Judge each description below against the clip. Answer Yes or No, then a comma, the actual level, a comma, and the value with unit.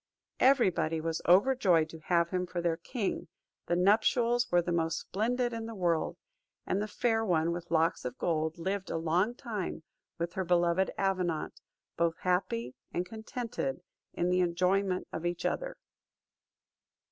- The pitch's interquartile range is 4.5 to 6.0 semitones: No, average, 3.8 semitones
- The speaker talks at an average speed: Yes, average, 160 wpm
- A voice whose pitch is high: No, medium, 180 Hz